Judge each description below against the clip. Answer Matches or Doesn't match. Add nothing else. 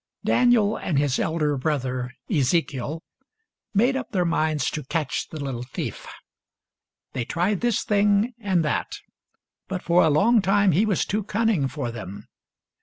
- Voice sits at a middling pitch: Matches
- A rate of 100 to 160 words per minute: Matches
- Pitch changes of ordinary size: Doesn't match